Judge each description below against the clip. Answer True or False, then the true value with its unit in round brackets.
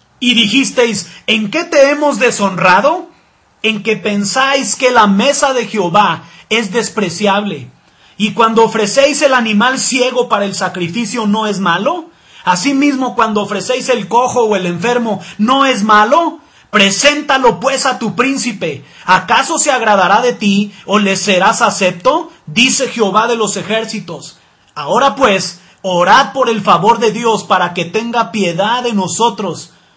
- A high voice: True (220 Hz)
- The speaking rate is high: False (145 wpm)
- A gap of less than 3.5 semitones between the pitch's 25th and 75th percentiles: False (4.1 semitones)